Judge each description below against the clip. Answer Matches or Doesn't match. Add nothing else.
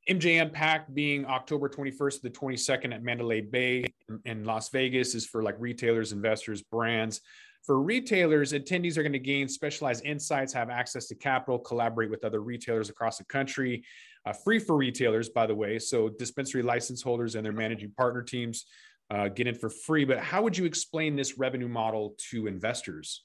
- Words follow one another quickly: Doesn't match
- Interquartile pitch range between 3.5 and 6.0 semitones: Matches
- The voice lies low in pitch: Matches